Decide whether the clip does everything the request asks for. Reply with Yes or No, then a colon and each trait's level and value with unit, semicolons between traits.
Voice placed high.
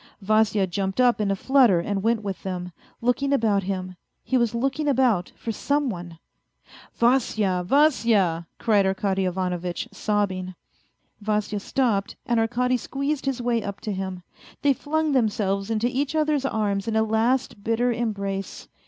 Yes: high, 215 Hz